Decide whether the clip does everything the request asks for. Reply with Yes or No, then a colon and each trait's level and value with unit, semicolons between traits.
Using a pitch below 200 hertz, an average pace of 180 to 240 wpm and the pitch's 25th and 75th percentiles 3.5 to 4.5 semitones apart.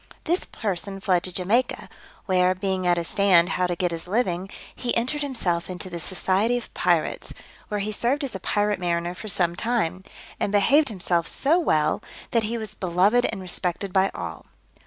Yes: high, 190 Hz; average, 185 wpm; average, 3.9 semitones